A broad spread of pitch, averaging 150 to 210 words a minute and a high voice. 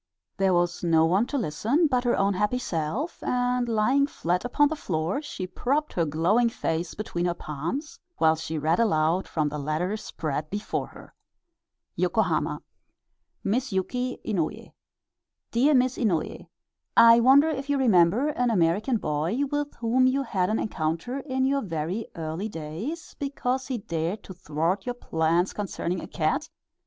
Yes: wide, 7.4 semitones; average, 160 wpm; high, 205 Hz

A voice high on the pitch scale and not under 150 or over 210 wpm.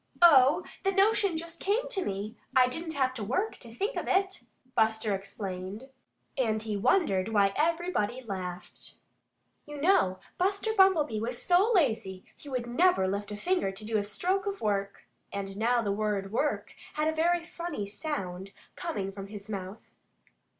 Yes: high, 240 Hz; average, 170 wpm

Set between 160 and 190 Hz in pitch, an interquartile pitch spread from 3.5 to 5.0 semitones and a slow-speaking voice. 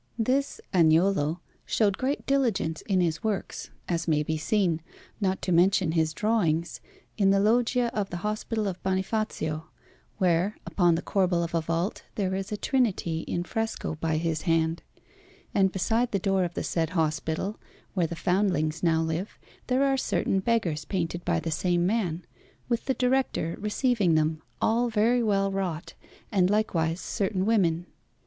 No: medium, 185 Hz; average, 4.4 semitones; average, 160 wpm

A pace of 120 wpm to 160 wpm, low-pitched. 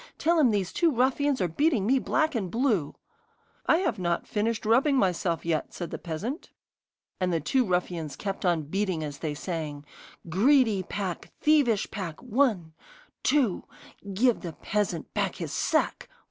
No: average, 155 wpm; high, 200 Hz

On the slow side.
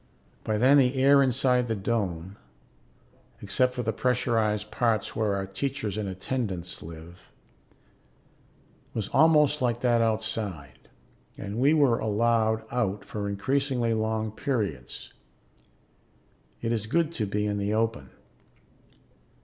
Yes: slow, 125 wpm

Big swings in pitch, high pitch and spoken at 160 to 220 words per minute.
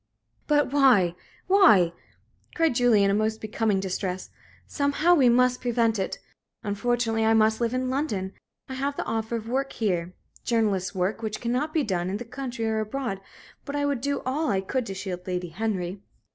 No: average, 4.8 semitones; high, 225 Hz; average, 185 wpm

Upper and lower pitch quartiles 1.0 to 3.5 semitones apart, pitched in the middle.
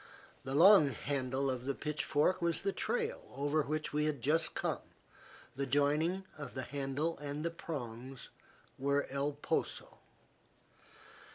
Yes: average, 2.9 semitones; medium, 145 Hz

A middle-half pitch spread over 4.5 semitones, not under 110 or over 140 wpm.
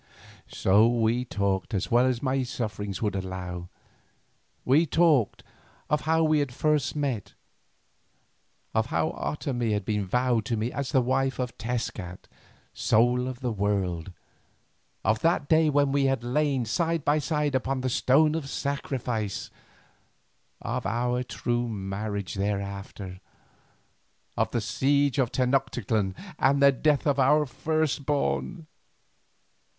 Yes: average, 4.9 semitones; slow, 135 wpm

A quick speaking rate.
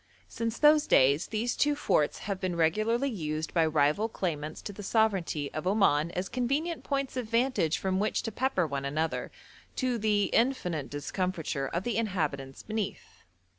No: average, 165 wpm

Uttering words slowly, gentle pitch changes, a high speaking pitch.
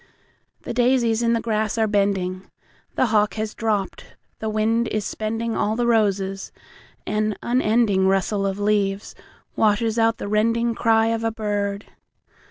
Yes: slow, 130 wpm; narrow, 2.0 semitones; high, 215 Hz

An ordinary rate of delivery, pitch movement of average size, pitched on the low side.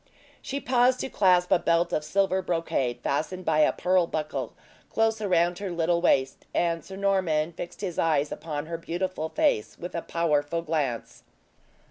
No: average, 165 wpm; average, 3.1 semitones; medium, 170 Hz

